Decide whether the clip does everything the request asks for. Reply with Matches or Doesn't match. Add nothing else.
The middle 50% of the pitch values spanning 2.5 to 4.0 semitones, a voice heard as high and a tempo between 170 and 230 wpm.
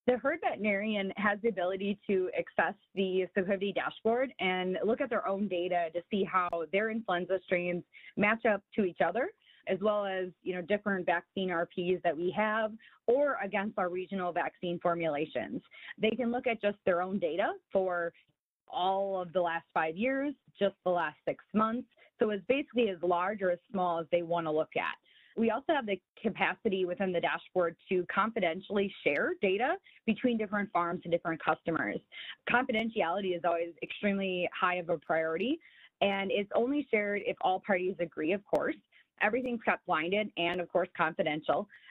Matches